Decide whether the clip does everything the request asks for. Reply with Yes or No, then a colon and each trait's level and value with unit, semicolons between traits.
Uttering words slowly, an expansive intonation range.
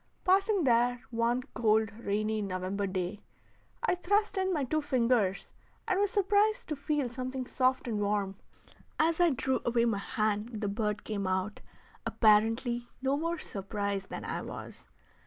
No: average, 155 wpm; wide, 5.8 semitones